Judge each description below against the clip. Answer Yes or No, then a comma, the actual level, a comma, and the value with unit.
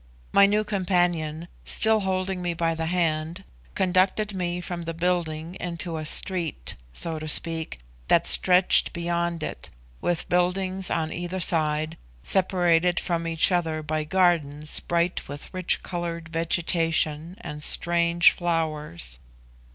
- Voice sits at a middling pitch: Yes, medium, 170 Hz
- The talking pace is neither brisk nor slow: No, slow, 130 wpm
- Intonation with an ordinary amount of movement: No, narrow, 2.0 semitones